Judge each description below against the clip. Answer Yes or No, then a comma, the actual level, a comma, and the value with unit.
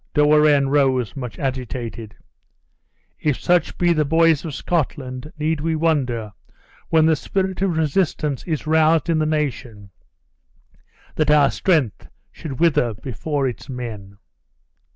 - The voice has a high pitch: No, medium, 150 Hz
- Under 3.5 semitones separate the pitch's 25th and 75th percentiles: No, average, 4.0 semitones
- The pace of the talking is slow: Yes, slow, 130 wpm